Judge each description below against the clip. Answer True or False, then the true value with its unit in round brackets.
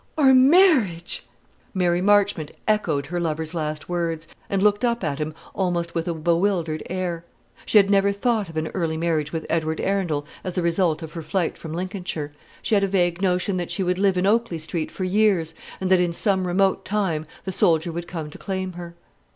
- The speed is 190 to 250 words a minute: True (200 wpm)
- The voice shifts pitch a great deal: False (3.2 semitones)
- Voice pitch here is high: False (175 Hz)